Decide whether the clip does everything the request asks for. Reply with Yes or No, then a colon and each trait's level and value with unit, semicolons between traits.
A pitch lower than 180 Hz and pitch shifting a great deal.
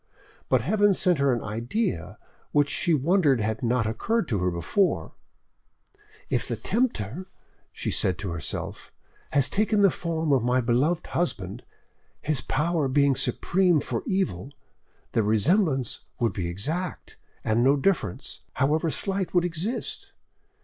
Yes: medium, 140 Hz; wide, 7.6 semitones